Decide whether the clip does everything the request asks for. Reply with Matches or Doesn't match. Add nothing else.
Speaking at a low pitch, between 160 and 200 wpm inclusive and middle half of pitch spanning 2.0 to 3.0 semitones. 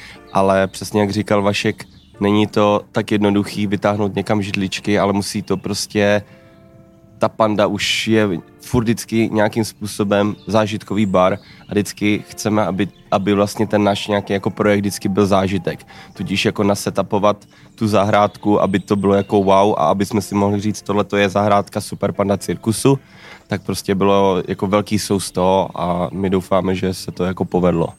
Doesn't match